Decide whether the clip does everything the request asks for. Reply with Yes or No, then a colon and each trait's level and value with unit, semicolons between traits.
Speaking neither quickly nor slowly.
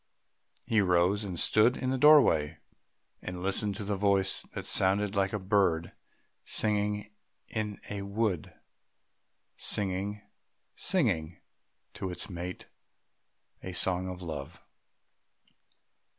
No: slow, 110 wpm